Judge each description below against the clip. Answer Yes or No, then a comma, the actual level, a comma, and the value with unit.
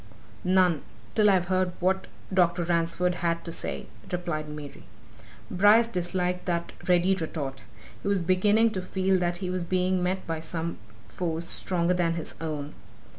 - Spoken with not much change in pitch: Yes, narrow, 1.8 semitones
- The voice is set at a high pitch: No, medium, 180 Hz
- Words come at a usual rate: Yes, average, 155 wpm